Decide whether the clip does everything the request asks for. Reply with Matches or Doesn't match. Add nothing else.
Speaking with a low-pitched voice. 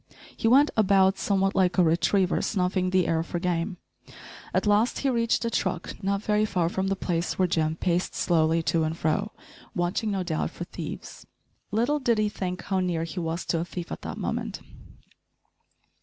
Doesn't match